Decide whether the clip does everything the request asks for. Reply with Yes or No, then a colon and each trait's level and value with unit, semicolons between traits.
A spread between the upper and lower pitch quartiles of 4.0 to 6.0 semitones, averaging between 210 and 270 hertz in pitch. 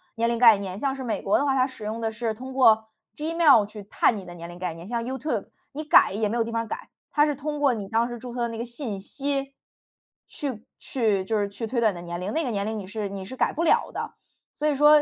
Yes: average, 4.6 semitones; high, 230 Hz